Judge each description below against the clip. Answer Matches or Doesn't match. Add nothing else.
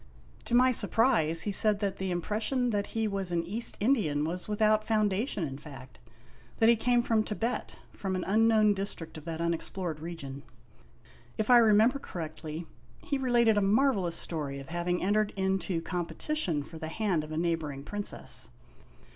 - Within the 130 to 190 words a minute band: Matches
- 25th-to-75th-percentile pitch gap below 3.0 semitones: Doesn't match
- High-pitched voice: Matches